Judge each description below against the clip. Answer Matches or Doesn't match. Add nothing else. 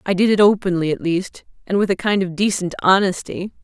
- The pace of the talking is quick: Matches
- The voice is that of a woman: Matches